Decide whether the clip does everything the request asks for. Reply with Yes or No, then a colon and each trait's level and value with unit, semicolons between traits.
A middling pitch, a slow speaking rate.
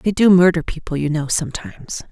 No: medium, 175 Hz; average, 200 wpm